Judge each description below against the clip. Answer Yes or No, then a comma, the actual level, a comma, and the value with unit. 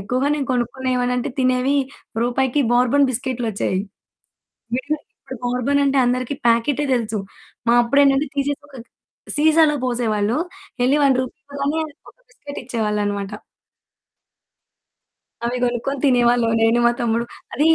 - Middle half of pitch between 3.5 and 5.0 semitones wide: No, average, 2.9 semitones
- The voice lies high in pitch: Yes, very high, 250 Hz